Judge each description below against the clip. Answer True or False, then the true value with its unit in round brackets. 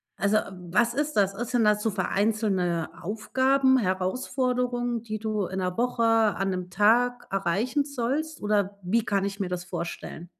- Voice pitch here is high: True (215 Hz)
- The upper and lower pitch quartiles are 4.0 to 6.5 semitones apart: True (4.3 semitones)